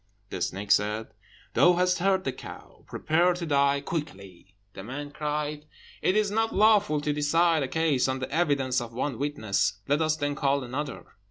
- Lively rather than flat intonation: No, average, 4.2 semitones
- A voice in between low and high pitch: Yes, medium, 145 Hz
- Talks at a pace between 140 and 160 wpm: No, average, 180 wpm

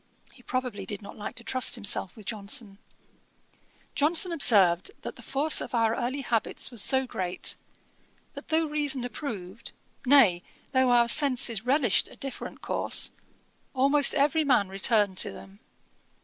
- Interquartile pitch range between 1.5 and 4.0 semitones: No, average, 5.3 semitones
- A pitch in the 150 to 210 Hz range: No, high, 245 Hz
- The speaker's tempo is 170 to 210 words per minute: No, average, 150 wpm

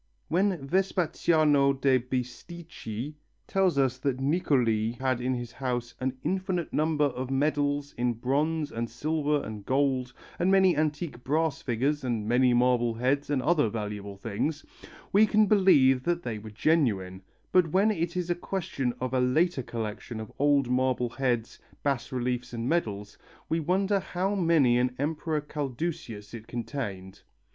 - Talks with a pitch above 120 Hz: Yes, low, 135 Hz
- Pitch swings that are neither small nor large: Yes, average, 4.8 semitones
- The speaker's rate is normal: Yes, average, 150 wpm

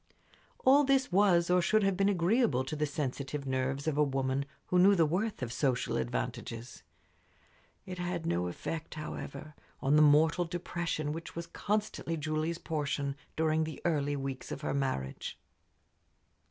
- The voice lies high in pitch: No, medium, 155 Hz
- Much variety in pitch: No, average, 4.2 semitones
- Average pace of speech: Yes, average, 155 wpm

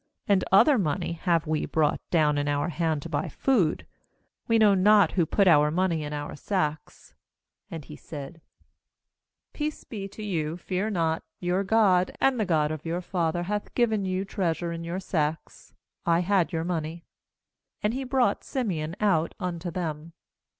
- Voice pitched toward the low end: No, medium, 175 Hz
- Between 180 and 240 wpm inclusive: No, average, 165 wpm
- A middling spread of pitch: Yes, average, 3.9 semitones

